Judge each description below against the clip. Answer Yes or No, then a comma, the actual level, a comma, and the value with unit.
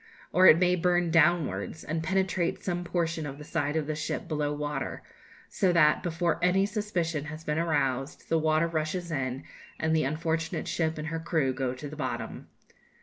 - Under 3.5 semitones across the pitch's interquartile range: Yes, narrow, 2.5 semitones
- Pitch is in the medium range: Yes, medium, 160 Hz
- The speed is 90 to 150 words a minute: No, average, 185 wpm